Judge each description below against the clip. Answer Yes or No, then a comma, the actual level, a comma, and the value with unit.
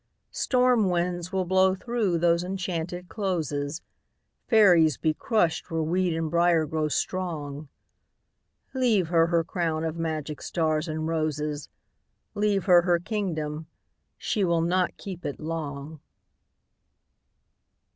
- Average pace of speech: No, slow, 115 wpm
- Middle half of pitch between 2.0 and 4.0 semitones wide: Yes, average, 2.9 semitones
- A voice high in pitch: No, medium, 170 Hz